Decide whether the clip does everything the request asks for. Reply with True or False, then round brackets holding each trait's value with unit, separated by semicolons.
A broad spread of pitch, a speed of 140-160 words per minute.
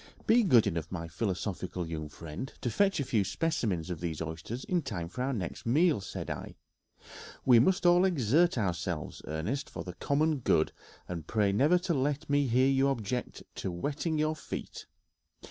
False (8.8 semitones; 175 wpm)